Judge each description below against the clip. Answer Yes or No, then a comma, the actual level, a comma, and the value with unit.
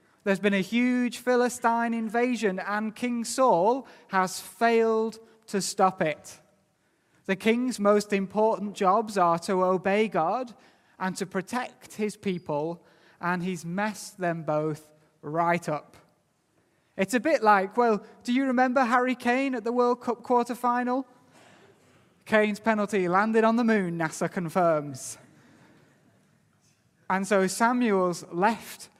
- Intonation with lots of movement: No, average, 4.2 semitones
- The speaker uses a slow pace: Yes, slow, 130 wpm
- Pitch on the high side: Yes, high, 205 Hz